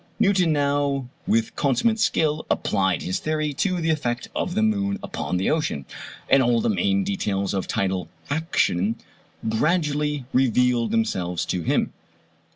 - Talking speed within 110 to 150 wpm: Yes, average, 145 wpm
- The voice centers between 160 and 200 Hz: No, medium, 145 Hz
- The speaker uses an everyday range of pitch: No, wide, 7.7 semitones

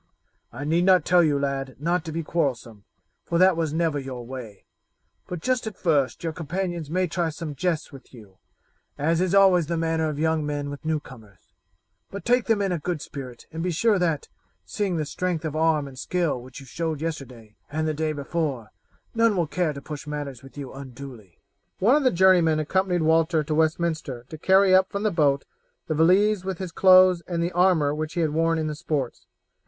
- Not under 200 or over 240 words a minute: Yes, fast, 205 wpm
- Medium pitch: Yes, medium, 160 Hz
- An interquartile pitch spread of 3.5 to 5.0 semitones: Yes, average, 3.9 semitones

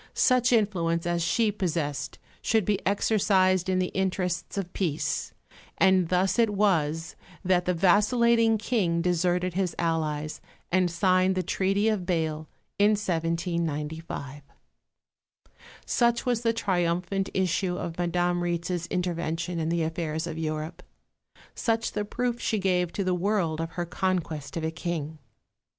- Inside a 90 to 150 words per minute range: Yes, average, 140 wpm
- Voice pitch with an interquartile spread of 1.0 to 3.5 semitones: Yes, average, 3.0 semitones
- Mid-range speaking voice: Yes, medium, 180 Hz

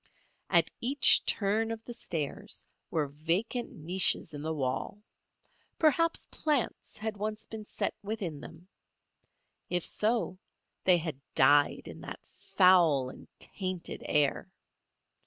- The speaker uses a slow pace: Yes, slow, 120 wpm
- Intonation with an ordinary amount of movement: No, wide, 6.0 semitones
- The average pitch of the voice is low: No, medium, 185 Hz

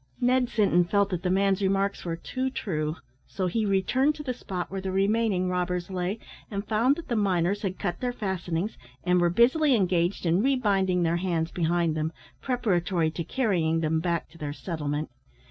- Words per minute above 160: Yes, average, 185 wpm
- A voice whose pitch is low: No, medium, 185 Hz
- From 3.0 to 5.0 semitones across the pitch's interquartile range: Yes, average, 3.7 semitones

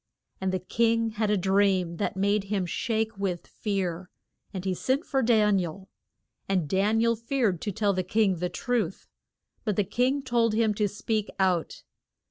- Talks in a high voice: Yes, high, 205 Hz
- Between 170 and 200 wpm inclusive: Yes, average, 185 wpm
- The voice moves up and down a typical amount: Yes, average, 3.1 semitones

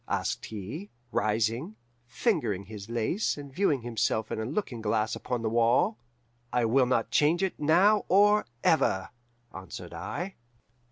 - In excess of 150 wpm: No, average, 145 wpm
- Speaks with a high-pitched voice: No, low, 120 Hz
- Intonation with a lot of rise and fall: Yes, wide, 7.8 semitones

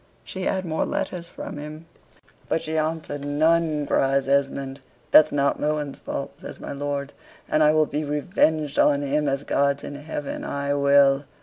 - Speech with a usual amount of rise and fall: No, narrow, 1.8 semitones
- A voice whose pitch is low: No, medium, 145 Hz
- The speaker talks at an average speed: Yes, average, 170 wpm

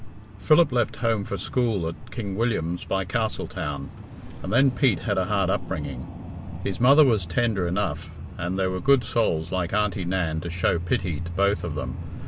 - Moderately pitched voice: No, very low, 95 Hz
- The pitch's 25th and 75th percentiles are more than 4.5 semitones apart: Yes, average, 5.1 semitones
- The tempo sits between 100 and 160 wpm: No, average, 185 wpm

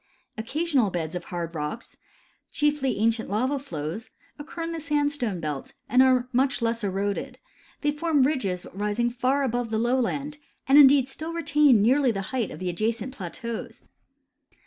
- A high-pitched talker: Yes, high, 245 Hz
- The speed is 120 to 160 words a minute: Yes, average, 155 wpm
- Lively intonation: Yes, wide, 5.7 semitones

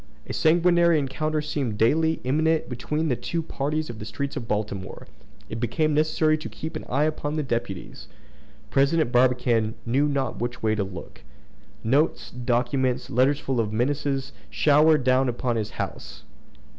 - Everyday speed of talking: Yes, average, 155 wpm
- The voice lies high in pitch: No, low, 135 Hz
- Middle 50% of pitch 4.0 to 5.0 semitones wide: Yes, average, 4.5 semitones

